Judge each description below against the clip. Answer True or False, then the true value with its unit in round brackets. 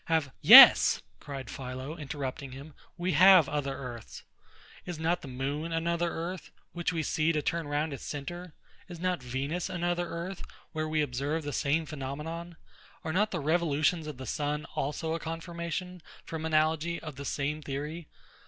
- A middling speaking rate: True (165 wpm)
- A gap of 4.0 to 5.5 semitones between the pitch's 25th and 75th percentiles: False (3.0 semitones)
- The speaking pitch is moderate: True (155 Hz)